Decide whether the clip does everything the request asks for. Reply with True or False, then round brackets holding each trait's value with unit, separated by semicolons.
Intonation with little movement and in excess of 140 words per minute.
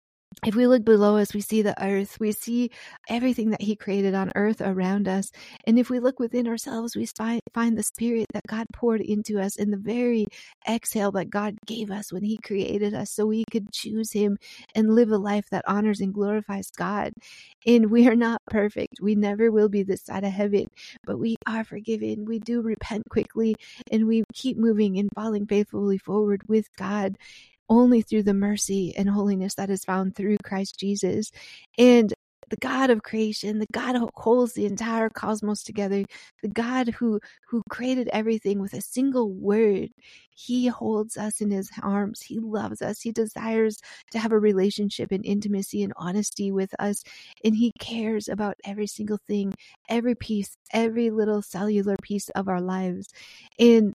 True (2.0 semitones; 180 wpm)